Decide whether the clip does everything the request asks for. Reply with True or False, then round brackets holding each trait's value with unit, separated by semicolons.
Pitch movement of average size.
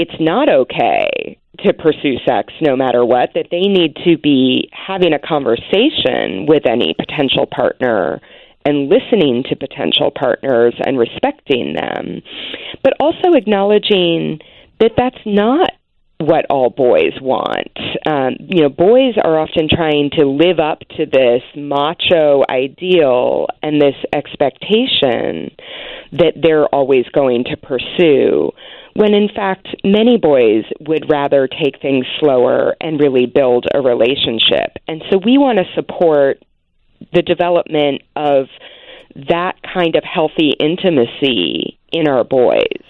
False (6.8 semitones)